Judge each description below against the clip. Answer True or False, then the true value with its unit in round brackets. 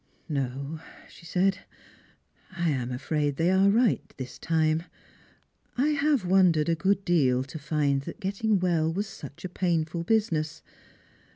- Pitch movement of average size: True (4.4 semitones)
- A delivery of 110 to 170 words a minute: True (135 wpm)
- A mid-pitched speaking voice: True (165 Hz)